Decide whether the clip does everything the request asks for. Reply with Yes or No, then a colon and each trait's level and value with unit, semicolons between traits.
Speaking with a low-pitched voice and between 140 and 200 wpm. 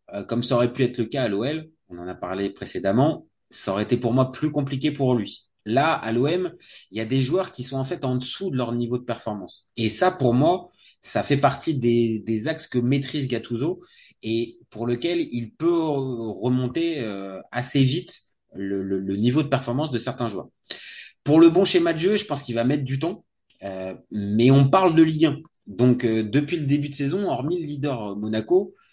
No: low, 125 Hz; average, 210 wpm